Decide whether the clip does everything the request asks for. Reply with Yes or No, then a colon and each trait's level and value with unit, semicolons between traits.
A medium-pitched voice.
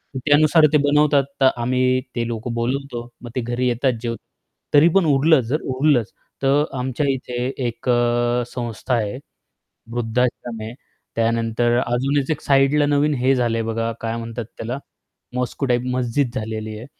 No: low, 125 Hz